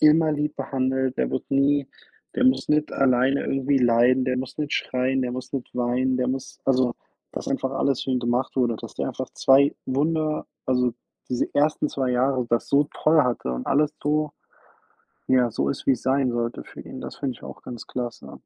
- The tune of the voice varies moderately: No, narrow, 2.3 semitones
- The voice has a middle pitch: No, low, 130 Hz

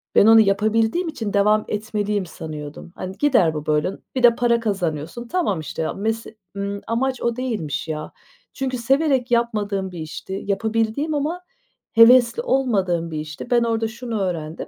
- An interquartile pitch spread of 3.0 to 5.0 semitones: Yes, average, 4.6 semitones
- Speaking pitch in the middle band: No, high, 220 Hz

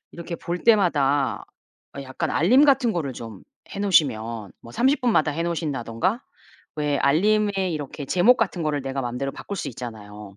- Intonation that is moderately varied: No, wide, 7.3 semitones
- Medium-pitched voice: Yes, medium, 150 Hz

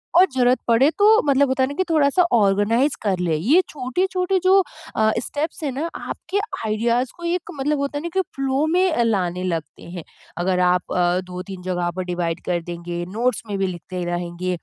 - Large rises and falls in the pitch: Yes, wide, 8.4 semitones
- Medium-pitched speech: No, high, 230 Hz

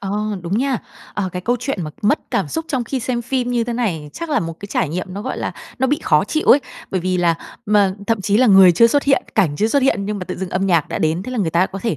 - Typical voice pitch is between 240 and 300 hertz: No, high, 205 Hz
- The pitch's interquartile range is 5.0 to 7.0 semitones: Yes, wide, 5.6 semitones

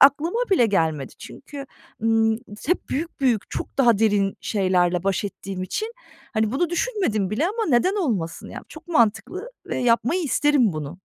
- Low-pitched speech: No, high, 230 Hz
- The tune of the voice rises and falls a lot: Yes, wide, 8.6 semitones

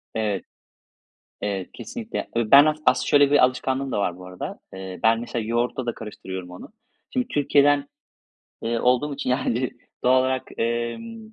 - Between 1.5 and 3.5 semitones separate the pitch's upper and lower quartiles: No, average, 4.4 semitones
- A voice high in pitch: No, low, 125 Hz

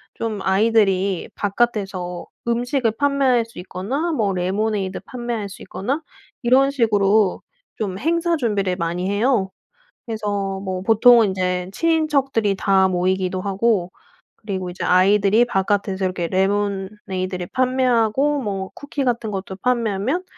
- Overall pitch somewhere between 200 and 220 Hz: Yes, high, 205 Hz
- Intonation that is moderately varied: Yes, average, 4.0 semitones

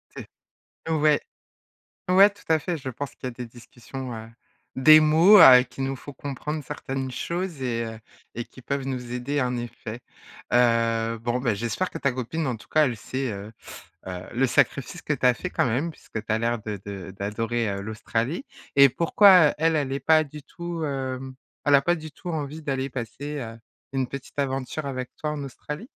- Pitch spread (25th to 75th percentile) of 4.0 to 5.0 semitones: Yes, average, 4.3 semitones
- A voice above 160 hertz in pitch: No, low, 130 Hz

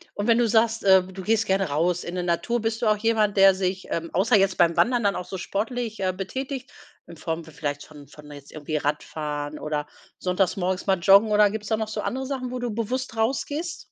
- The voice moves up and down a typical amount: Yes, average, 4.7 semitones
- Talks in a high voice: Yes, high, 195 Hz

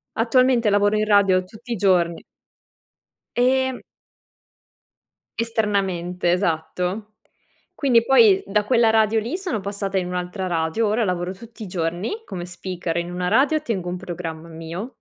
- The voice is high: Yes, high, 200 Hz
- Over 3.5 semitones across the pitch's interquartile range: Yes, average, 4.3 semitones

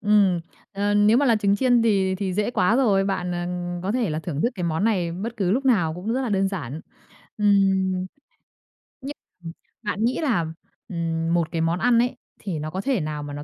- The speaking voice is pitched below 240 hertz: Yes, high, 195 Hz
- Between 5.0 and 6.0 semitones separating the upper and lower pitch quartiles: No, average, 4.3 semitones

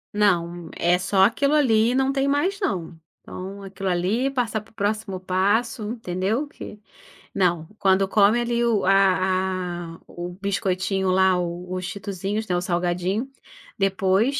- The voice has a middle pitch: No, high, 195 Hz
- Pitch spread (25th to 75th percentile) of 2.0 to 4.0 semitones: Yes, average, 3.4 semitones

